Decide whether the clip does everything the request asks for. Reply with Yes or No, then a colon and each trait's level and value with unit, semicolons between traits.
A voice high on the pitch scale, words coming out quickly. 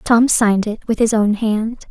Yes: high, 220 Hz; fast, 220 wpm